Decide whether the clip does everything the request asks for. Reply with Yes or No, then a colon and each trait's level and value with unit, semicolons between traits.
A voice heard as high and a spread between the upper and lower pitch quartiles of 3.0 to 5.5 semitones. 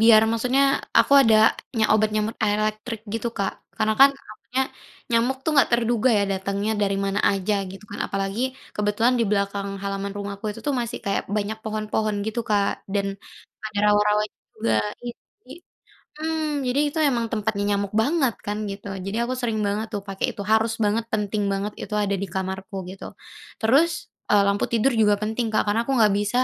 No: high, 215 Hz; narrow, 2.4 semitones